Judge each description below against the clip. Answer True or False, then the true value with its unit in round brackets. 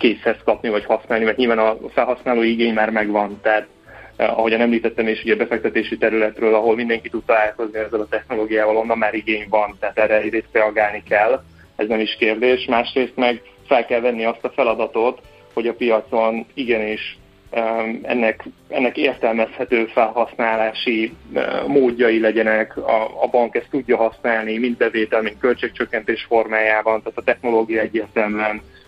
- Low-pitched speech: True (110 Hz)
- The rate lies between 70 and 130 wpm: False (150 wpm)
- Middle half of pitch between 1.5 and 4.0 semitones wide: False (1.1 semitones)